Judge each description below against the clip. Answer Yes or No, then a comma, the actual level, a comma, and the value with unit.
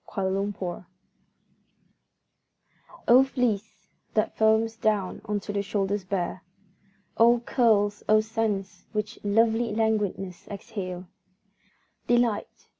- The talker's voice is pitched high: Yes, high, 210 Hz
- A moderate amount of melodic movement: No, narrow, 2.2 semitones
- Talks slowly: Yes, slow, 95 wpm